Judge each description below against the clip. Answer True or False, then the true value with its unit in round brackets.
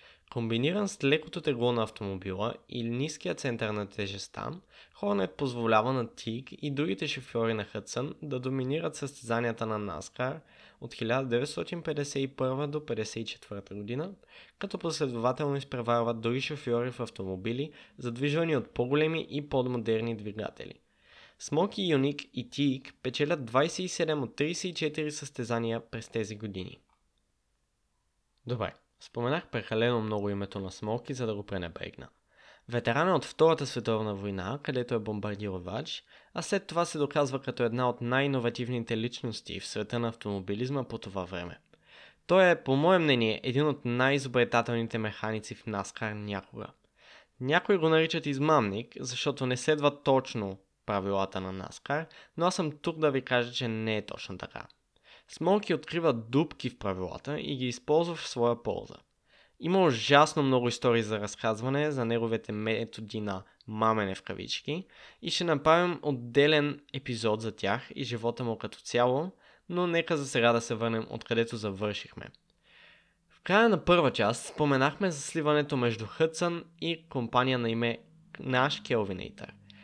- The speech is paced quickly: False (140 wpm)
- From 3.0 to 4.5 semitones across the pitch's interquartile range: False (4.9 semitones)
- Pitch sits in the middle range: False (125 Hz)